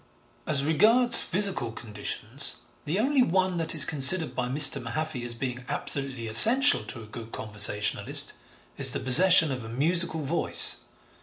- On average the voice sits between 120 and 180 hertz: Yes, medium, 140 Hz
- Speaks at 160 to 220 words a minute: No, average, 150 wpm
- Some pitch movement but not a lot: No, wide, 6.8 semitones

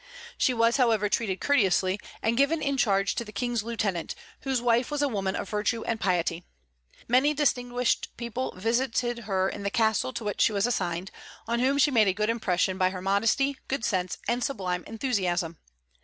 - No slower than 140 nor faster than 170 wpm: No, average, 185 wpm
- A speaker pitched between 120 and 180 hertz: No, high, 225 Hz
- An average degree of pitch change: Yes, average, 4.3 semitones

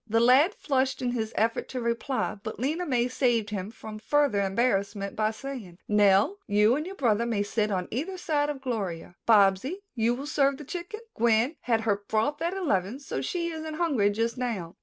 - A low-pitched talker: No, high, 235 Hz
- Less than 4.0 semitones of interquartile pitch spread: No, wide, 5.4 semitones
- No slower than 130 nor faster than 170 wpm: No, average, 195 wpm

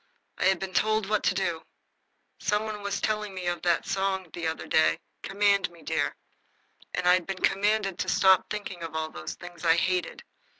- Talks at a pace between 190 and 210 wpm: Yes, average, 195 wpm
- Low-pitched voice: No, high, 190 Hz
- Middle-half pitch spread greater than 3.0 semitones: No, average, 2.7 semitones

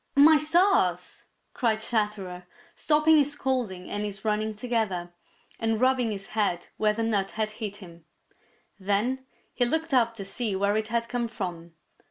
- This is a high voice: Yes, high, 220 Hz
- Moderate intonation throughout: Yes, average, 3.8 semitones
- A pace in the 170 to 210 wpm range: No, average, 160 wpm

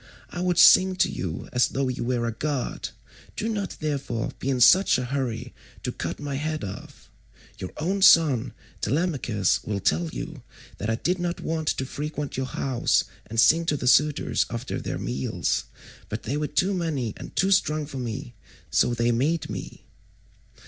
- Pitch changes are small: No, wide, 5.4 semitones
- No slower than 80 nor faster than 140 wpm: No, average, 180 wpm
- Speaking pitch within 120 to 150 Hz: Yes, medium, 140 Hz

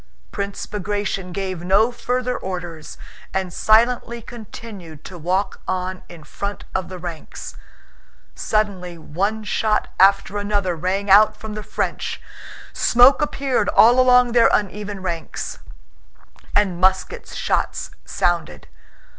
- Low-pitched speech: No, high, 200 Hz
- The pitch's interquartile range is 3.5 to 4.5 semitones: No, average, 3.1 semitones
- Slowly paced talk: Yes, slow, 120 wpm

